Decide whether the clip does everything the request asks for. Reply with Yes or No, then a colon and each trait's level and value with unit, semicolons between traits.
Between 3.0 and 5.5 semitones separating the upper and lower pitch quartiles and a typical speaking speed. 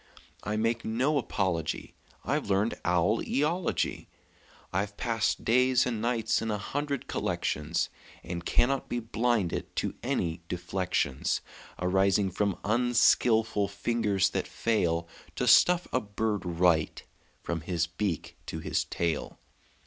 No: average, 4.8 semitones; slow, 125 wpm